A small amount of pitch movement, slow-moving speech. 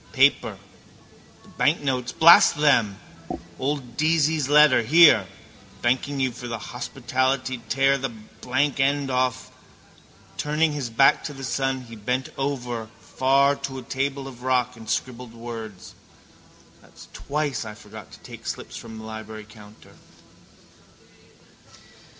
No: average, 3.1 semitones; slow, 130 wpm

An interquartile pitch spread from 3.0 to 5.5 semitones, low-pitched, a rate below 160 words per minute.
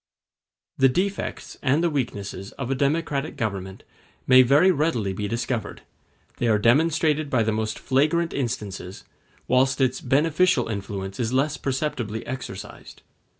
Yes: average, 5.2 semitones; low, 130 Hz; slow, 135 wpm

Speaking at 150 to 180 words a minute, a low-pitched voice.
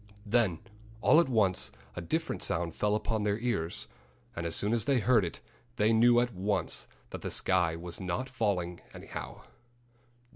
Yes: average, 170 wpm; low, 105 Hz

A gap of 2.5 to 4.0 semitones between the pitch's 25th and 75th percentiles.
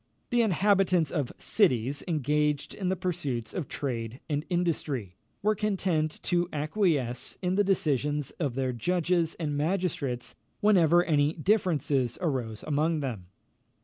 No: average, 4.8 semitones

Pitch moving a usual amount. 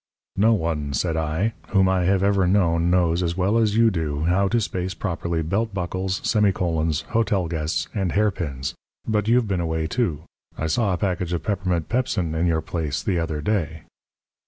Yes: average, 3.7 semitones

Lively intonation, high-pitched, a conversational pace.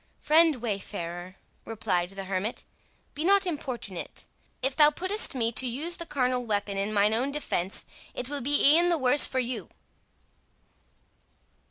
Yes: wide, 6.6 semitones; very high, 250 Hz; average, 150 wpm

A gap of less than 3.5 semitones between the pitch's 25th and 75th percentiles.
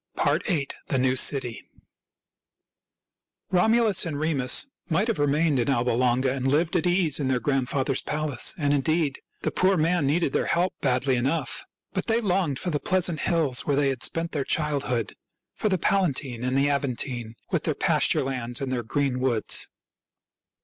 No: average, 4.4 semitones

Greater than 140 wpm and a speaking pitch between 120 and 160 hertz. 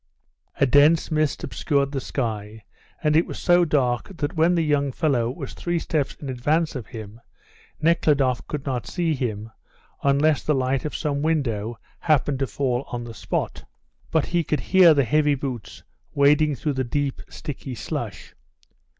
Yes: average, 165 wpm; medium, 140 Hz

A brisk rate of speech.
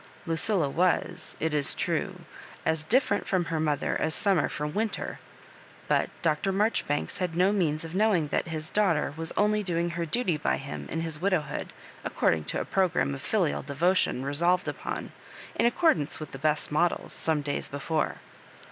No: average, 175 wpm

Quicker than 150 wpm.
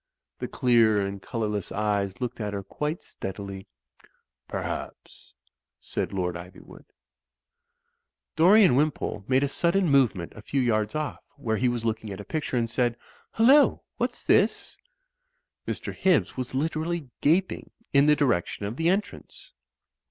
No: average, 145 wpm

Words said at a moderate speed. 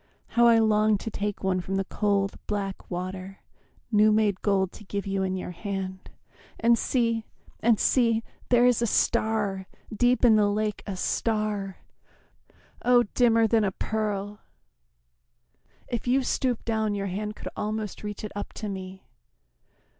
Yes: average, 155 wpm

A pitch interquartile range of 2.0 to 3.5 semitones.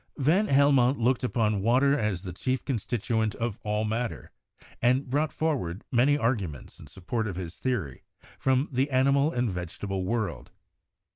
No: average, 4.4 semitones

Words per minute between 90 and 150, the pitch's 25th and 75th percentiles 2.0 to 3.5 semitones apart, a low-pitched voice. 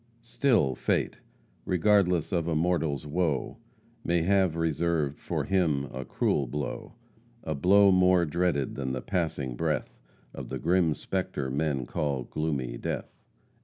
No: slow, 135 wpm; average, 4.4 semitones; very low, 80 Hz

